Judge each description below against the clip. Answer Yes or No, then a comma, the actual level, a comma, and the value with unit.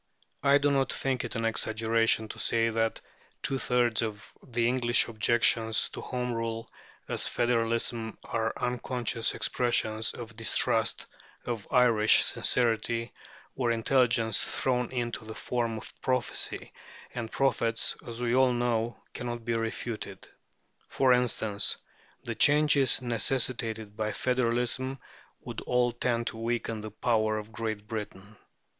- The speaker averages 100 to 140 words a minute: Yes, slow, 135 wpm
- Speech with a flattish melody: Yes, narrow, 1.7 semitones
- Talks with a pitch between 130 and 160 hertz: No, low, 115 Hz